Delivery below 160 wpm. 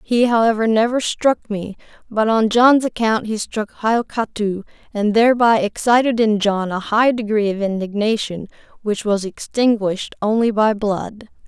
Yes: average, 145 wpm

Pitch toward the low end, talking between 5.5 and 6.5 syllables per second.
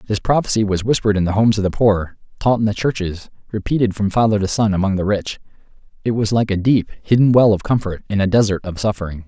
Yes: low, 105 Hz; 6.4 syllables/s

